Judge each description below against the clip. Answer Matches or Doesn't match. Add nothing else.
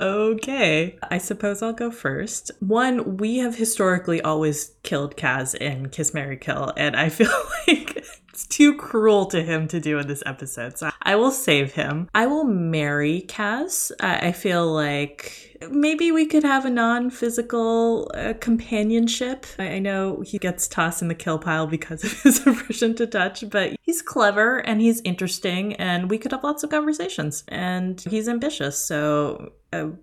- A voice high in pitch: Matches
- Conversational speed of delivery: Matches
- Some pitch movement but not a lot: Doesn't match